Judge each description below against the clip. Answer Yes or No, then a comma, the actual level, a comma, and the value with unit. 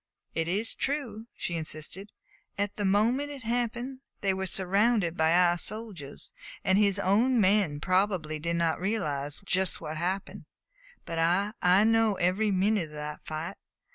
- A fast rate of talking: No, average, 155 wpm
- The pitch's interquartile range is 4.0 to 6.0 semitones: Yes, average, 4.3 semitones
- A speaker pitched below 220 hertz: Yes, high, 190 Hz